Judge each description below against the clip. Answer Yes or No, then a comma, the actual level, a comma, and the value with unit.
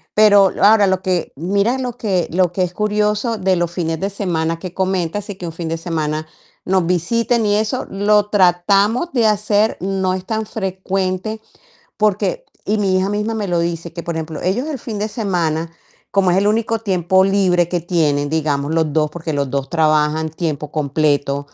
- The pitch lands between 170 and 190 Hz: Yes, medium, 185 Hz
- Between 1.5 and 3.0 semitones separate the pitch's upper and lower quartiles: No, average, 4.1 semitones